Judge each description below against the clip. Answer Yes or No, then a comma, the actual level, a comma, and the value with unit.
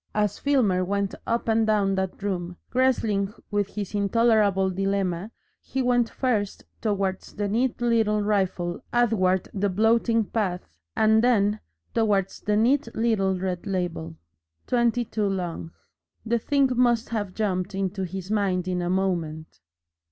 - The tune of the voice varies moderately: Yes, average, 3.2 semitones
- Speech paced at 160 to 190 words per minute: No, slow, 135 wpm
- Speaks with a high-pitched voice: Yes, high, 205 Hz